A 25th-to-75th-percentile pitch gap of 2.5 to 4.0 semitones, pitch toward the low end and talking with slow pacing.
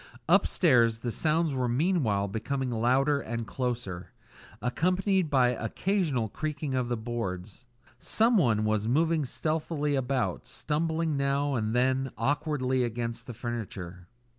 No: average, 4.6 semitones; low, 130 Hz; slow, 120 wpm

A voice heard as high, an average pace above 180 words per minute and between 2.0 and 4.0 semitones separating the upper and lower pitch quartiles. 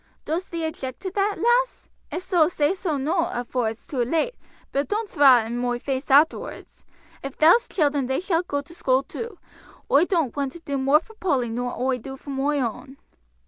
No: very high, 285 Hz; fast, 205 wpm; average, 4.9 semitones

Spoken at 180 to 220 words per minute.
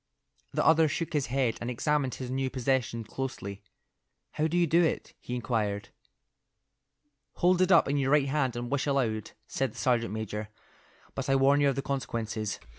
Yes: average, 185 wpm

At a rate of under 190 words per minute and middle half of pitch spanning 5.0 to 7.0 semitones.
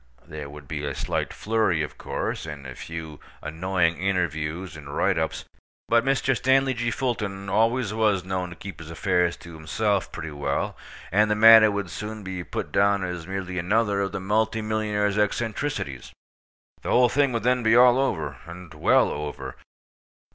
Yes: average, 175 wpm; average, 5.3 semitones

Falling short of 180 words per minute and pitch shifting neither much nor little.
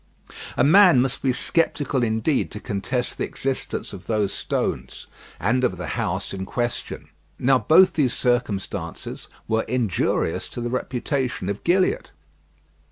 Yes: average, 140 wpm; average, 4.2 semitones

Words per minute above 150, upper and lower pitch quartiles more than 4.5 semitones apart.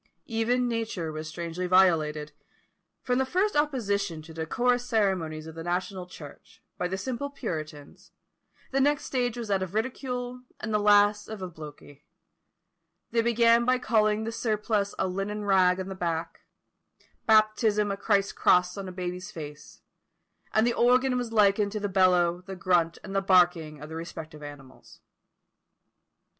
Yes: average, 160 wpm; average, 4.9 semitones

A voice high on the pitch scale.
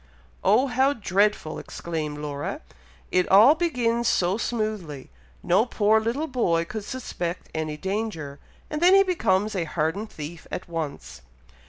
Yes: high, 200 Hz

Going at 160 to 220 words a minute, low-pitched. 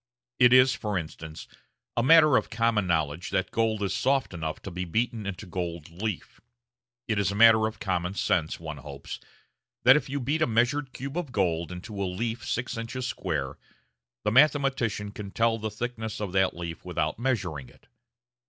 Yes: average, 180 wpm; low, 105 Hz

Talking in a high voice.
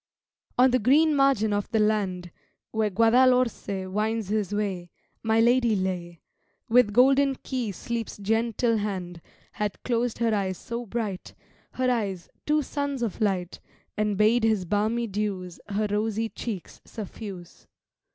Yes: high, 215 Hz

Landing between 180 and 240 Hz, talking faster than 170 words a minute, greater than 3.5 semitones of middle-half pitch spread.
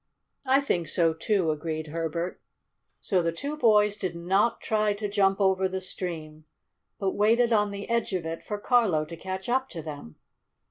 Yes: high, 190 Hz; average, 180 wpm; average, 4.2 semitones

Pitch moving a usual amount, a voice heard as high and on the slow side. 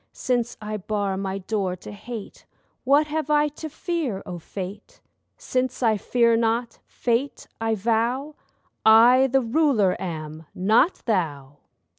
Yes: average, 4.9 semitones; high, 225 Hz; slow, 130 wpm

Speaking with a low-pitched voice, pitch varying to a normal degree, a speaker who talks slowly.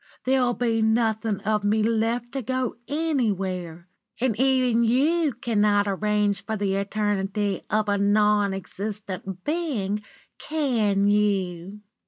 No: high, 210 Hz; average, 3.1 semitones; slow, 120 wpm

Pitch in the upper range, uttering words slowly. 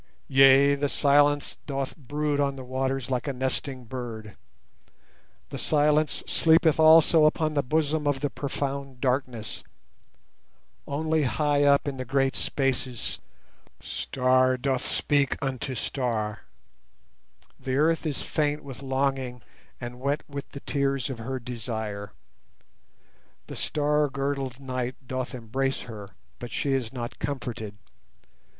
No: low, 135 Hz; slow, 130 wpm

